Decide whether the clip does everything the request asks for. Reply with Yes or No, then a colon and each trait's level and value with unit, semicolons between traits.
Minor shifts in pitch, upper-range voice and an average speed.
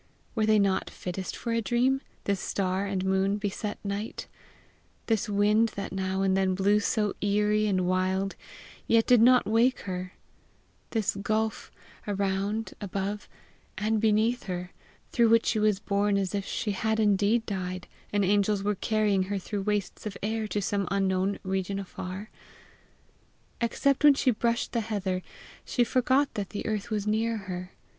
Yes: narrow, 2.2 semitones; high, 205 Hz; average, 160 wpm